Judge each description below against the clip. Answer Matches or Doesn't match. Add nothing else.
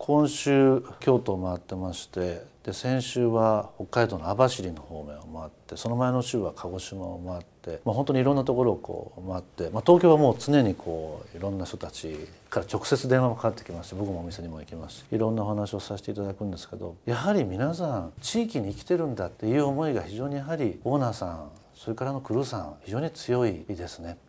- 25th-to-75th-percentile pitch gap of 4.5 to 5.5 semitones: Doesn't match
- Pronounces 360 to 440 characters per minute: Matches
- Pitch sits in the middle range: Doesn't match